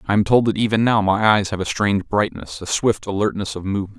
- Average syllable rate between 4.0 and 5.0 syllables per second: No, 6.2 syllables/s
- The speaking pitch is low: Yes, low, 100 Hz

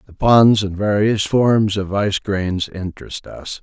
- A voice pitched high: No, low, 100 Hz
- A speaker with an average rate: Yes, average, 165 wpm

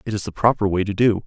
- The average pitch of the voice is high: No, low, 105 Hz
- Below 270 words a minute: No, fast, 335 wpm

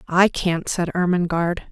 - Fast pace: No, average, 140 wpm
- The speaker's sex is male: No, female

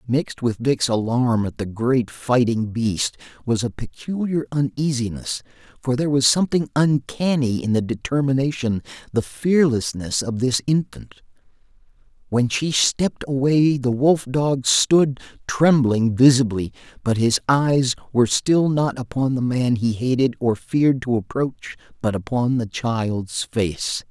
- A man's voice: Yes, male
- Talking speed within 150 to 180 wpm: No, average, 140 wpm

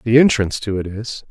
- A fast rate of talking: Yes, fast, 230 wpm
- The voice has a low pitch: Yes, low, 115 Hz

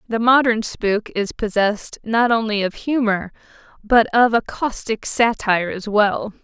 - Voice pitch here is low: No, high, 215 Hz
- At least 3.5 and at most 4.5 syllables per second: Yes, 4.3 syllables/s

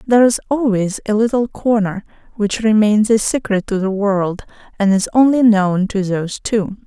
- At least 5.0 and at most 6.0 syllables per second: No, 4.7 syllables/s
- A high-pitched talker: Yes, high, 215 Hz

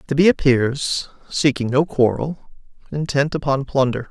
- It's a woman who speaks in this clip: No, male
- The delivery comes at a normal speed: No, slow, 130 wpm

